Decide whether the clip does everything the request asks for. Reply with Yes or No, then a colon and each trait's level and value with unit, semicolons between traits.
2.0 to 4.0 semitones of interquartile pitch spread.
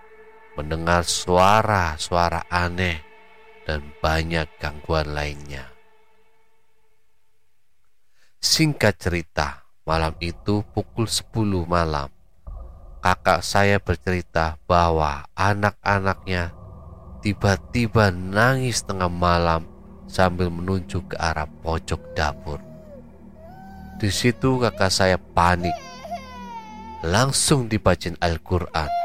No: average, 4.6 semitones